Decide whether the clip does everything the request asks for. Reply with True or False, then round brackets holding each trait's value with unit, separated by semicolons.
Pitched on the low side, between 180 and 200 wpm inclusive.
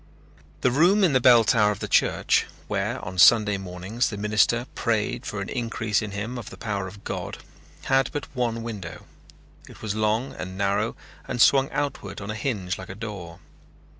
True (110 Hz; 190 wpm)